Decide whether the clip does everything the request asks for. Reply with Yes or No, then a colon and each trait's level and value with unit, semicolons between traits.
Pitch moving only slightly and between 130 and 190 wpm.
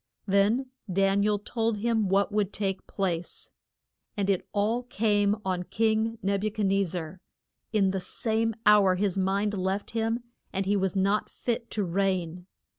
Yes: narrow, 2.2 semitones; average, 170 wpm